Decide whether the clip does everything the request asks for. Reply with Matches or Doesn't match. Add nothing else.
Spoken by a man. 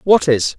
Matches